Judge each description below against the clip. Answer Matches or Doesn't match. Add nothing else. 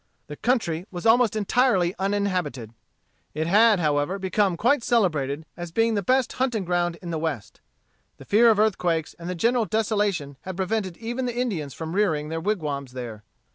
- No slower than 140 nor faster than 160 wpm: Doesn't match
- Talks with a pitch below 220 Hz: Matches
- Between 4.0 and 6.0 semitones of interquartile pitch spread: Matches